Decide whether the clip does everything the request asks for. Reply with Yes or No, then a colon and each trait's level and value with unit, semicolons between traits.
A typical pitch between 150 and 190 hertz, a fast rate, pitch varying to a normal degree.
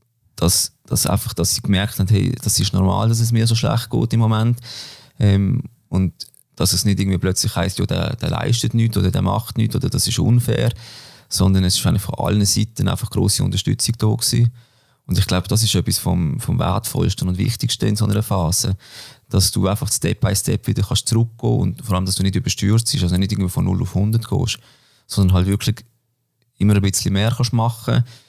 No: low, 110 Hz; fast, 220 wpm; average, 3.6 semitones